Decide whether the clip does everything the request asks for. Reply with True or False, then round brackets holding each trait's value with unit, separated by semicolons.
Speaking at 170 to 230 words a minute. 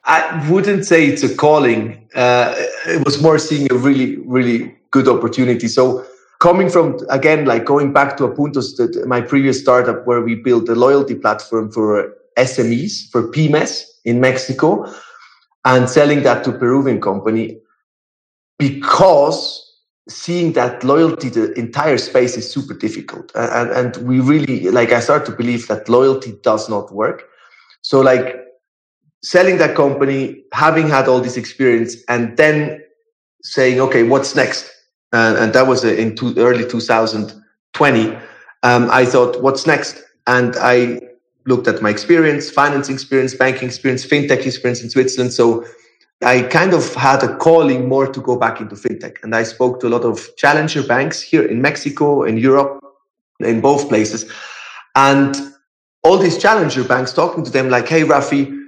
False (155 wpm)